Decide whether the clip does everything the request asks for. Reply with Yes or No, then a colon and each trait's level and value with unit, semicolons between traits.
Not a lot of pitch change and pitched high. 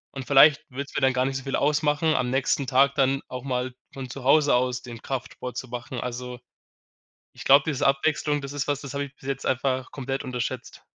No: narrow, 1.7 semitones; low, 135 Hz